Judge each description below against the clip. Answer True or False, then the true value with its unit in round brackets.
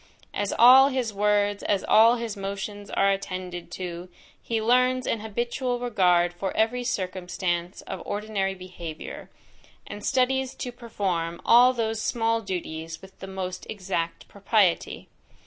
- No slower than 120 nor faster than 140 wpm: True (135 wpm)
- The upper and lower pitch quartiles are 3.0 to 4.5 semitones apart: True (4.2 semitones)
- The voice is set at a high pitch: True (205 Hz)